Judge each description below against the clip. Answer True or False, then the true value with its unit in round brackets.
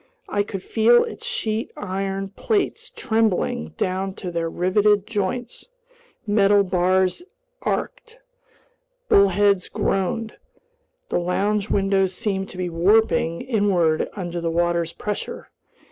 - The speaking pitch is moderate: False (195 Hz)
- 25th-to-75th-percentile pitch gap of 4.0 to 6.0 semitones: False (2.7 semitones)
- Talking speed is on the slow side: True (115 wpm)